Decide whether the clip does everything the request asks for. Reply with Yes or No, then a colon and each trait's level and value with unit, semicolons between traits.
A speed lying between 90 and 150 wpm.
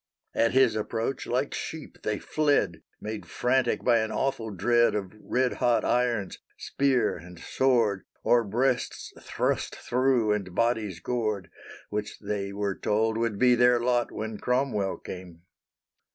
Yes: average, 140 wpm